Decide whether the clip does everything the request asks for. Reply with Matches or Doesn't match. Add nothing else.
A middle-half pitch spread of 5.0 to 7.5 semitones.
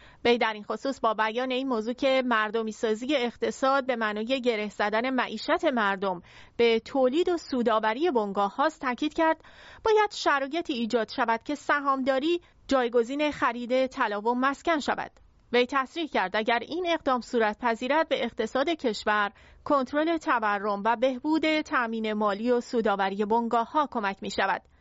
Doesn't match